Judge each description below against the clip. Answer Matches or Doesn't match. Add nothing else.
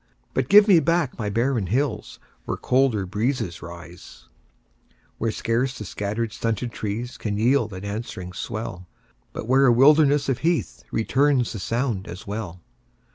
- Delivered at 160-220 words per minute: Doesn't match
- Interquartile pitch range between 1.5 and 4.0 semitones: Doesn't match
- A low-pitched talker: Matches